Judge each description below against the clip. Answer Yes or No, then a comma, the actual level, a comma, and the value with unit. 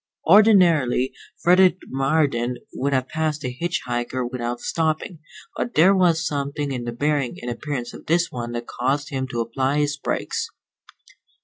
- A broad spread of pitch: No, average, 4.3 semitones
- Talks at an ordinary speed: Yes, average, 155 wpm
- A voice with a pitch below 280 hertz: Yes, medium, 140 Hz